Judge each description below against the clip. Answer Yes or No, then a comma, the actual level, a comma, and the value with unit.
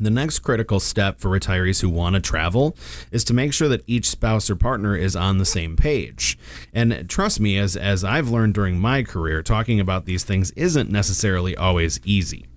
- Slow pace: No, average, 200 wpm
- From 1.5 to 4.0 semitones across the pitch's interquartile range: Yes, average, 3.7 semitones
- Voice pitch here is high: No, low, 100 Hz